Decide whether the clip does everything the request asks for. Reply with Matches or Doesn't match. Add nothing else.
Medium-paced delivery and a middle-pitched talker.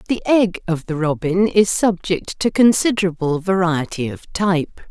Matches